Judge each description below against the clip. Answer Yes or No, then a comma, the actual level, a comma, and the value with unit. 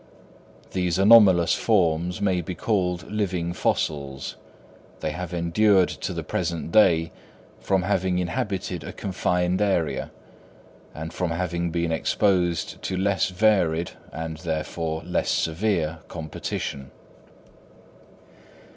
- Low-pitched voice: Yes, very low, 90 Hz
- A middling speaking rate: No, slow, 110 wpm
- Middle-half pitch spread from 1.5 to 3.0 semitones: Yes, narrow, 2.6 semitones